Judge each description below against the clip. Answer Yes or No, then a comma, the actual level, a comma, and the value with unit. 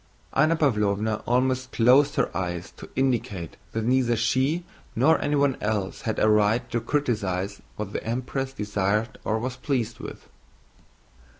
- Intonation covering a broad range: No, average, 3.8 semitones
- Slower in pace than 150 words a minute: Yes, average, 140 wpm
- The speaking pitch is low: Yes, low, 115 Hz